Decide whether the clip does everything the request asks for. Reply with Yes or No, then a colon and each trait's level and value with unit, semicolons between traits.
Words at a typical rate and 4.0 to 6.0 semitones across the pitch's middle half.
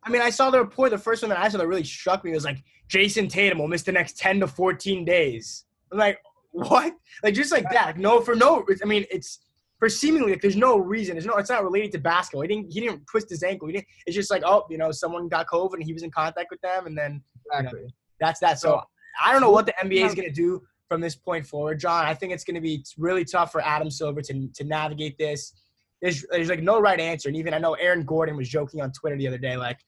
No: fast, 275 wpm; average, 4.5 semitones